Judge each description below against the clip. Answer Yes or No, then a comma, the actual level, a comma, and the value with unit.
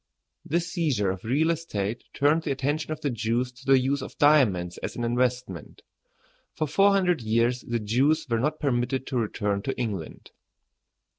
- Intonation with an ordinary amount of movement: Yes, average, 4.8 semitones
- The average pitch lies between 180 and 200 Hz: No, low, 125 Hz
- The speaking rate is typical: Yes, average, 170 wpm